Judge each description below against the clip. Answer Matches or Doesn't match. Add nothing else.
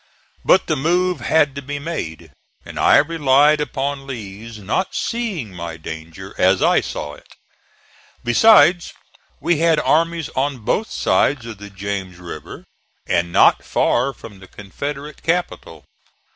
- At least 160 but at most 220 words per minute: Doesn't match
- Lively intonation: Matches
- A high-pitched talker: Doesn't match